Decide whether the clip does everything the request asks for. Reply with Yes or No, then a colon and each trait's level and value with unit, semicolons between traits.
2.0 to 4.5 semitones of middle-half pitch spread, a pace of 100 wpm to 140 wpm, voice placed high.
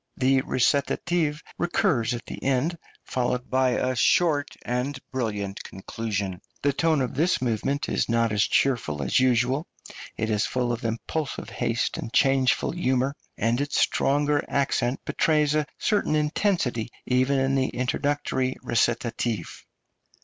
No: average, 3.4 semitones; slow, 135 wpm; low, 130 Hz